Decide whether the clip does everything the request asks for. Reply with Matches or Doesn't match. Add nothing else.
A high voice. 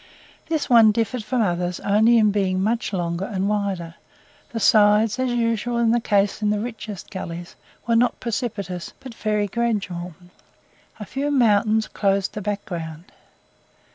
Matches